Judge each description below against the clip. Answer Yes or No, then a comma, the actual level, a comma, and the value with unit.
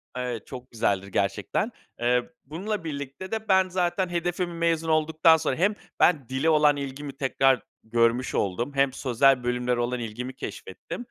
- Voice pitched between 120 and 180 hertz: Yes, medium, 140 Hz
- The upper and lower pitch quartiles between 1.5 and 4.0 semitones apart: No, average, 5.1 semitones